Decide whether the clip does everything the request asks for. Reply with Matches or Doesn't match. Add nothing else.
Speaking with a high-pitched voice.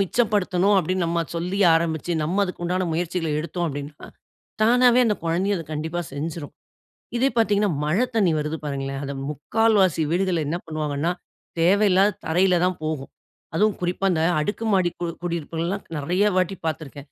Doesn't match